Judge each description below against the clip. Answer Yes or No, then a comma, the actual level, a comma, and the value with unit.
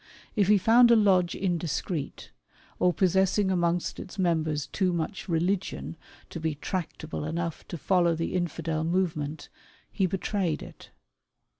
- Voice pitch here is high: No, medium, 175 Hz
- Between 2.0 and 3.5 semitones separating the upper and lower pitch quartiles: Yes, average, 2.8 semitones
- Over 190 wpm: No, slow, 135 wpm